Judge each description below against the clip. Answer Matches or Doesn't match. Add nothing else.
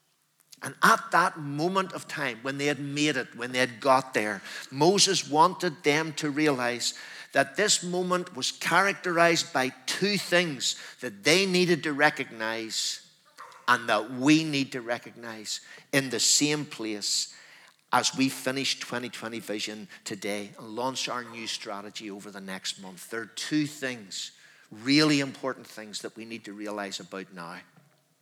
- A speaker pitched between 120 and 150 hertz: Matches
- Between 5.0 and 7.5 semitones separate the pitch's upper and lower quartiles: Matches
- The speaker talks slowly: Doesn't match